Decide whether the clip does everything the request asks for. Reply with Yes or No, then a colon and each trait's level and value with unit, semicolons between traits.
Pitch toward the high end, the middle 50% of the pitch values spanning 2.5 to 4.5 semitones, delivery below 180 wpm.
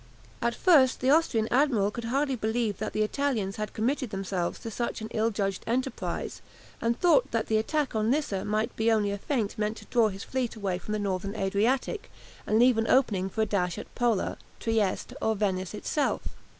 No: high, 220 Hz; average, 3.6 semitones; average, 200 wpm